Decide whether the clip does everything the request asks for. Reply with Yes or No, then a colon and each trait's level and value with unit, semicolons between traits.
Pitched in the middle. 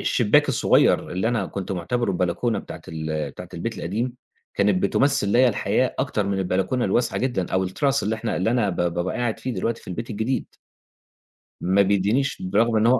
No: low, 105 Hz